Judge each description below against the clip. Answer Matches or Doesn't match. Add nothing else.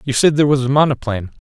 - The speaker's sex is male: Matches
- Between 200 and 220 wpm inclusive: Doesn't match